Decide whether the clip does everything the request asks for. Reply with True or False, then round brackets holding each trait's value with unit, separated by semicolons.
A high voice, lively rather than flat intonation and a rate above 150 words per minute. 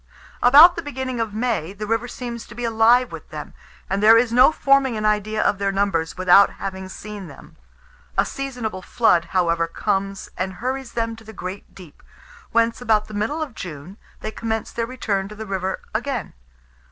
False (220 Hz; 3.7 semitones; 190 wpm)